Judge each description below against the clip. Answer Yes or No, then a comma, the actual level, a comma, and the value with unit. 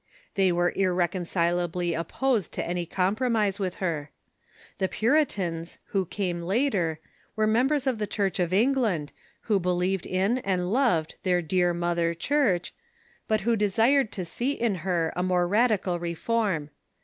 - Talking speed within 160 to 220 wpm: No, average, 150 wpm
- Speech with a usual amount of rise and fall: Yes, average, 4.1 semitones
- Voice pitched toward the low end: No, medium, 185 Hz